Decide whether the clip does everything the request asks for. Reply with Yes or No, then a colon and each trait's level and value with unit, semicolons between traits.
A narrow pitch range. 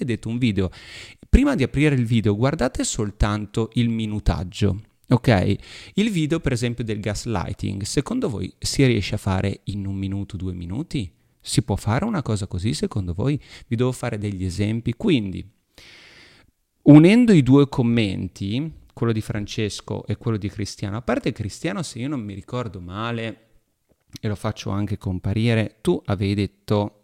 No: average, 3.6 semitones